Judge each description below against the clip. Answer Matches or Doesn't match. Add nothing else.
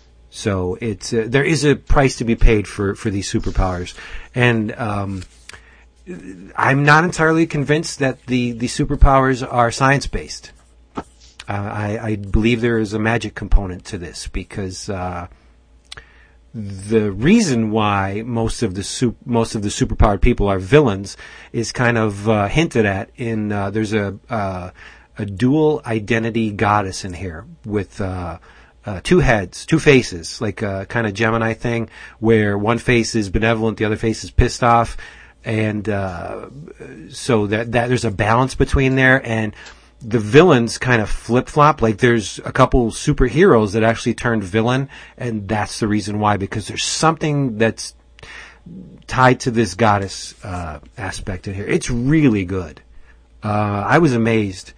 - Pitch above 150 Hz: Doesn't match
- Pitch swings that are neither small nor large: Matches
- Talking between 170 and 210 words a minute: Doesn't match